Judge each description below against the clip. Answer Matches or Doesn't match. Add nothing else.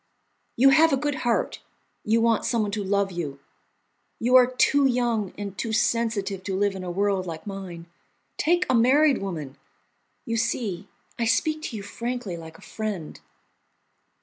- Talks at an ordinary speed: Matches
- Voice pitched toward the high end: Matches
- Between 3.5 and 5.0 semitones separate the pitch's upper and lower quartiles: Matches